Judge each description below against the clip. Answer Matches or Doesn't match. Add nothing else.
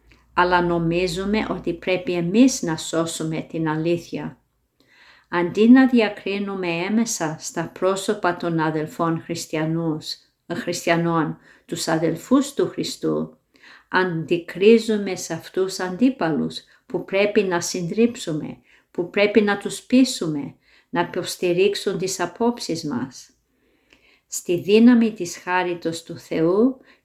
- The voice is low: Doesn't match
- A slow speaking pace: Matches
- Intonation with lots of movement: Doesn't match